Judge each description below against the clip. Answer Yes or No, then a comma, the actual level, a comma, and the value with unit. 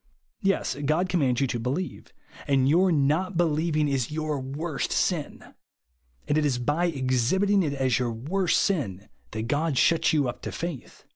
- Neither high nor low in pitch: Yes, medium, 150 Hz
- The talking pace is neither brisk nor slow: Yes, average, 170 wpm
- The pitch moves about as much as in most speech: Yes, average, 4.6 semitones